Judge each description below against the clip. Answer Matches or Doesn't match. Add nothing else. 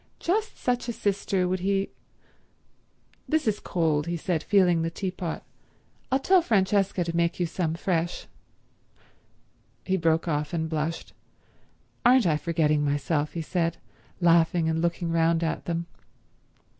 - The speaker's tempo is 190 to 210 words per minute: Doesn't match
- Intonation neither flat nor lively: Matches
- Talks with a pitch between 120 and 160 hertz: Doesn't match